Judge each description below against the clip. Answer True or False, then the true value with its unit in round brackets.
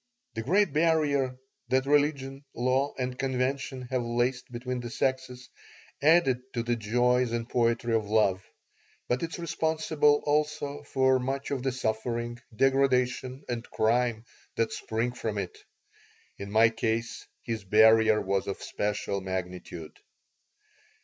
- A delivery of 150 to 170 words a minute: False (135 wpm)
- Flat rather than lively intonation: False (3.1 semitones)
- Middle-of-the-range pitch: False (125 Hz)